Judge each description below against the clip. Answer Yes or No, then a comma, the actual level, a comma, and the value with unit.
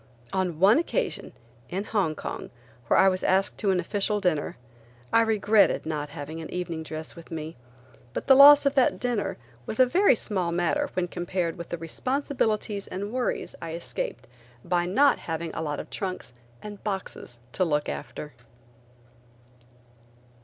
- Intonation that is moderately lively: Yes, average, 4.9 semitones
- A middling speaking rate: Yes, average, 155 wpm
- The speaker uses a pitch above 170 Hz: Yes, medium, 185 Hz